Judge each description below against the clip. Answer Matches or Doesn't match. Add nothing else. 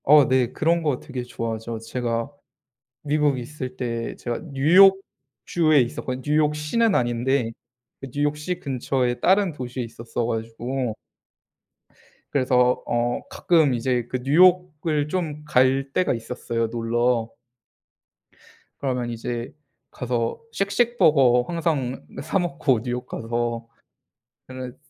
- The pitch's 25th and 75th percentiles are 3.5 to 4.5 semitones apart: Matches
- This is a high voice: Doesn't match